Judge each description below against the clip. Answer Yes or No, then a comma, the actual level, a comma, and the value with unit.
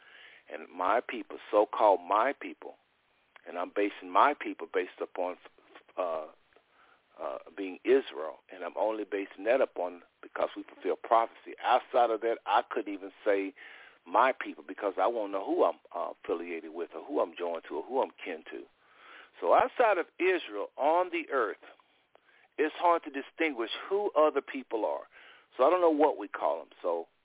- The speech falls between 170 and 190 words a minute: Yes, average, 175 wpm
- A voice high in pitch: Yes, very high, 340 Hz